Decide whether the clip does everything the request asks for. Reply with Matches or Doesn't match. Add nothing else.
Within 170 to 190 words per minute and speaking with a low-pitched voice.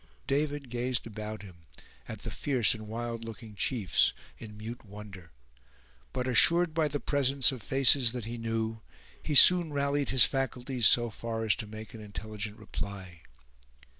Doesn't match